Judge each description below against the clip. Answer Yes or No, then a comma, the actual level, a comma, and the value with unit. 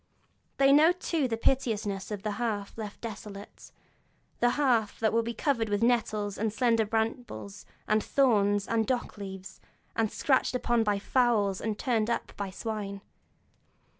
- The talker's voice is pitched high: Yes, high, 220 Hz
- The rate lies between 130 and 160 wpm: Yes, average, 155 wpm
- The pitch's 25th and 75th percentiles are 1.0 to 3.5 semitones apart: Yes, average, 2.8 semitones